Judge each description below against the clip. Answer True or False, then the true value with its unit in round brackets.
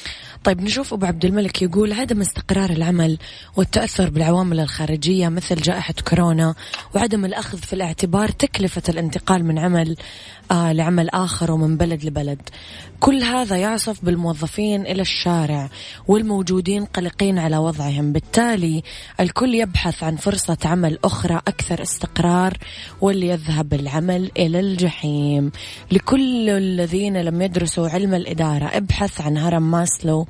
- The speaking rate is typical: False (120 wpm)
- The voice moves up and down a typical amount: True (3.1 semitones)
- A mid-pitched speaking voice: True (175 Hz)